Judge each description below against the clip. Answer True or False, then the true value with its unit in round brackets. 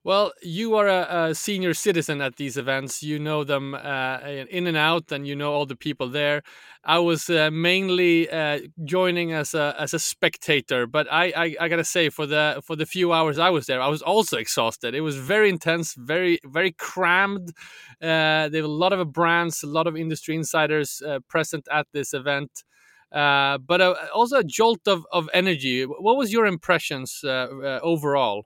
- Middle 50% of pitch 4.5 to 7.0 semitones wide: False (3.1 semitones)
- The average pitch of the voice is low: False (160 Hz)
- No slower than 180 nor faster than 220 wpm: True (200 wpm)